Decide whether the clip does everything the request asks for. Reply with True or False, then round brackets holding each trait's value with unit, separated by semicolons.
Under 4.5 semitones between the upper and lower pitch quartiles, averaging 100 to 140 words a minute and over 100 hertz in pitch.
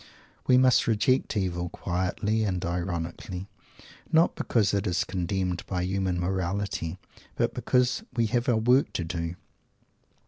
False (4.0 semitones; 135 wpm; 95 Hz)